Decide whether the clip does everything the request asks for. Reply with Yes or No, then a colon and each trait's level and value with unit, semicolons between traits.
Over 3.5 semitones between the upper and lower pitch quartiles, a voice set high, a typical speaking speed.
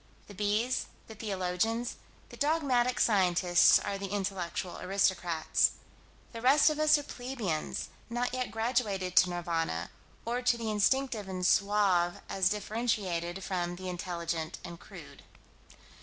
No: average, 4.9 semitones; high, 200 Hz; slow, 130 wpm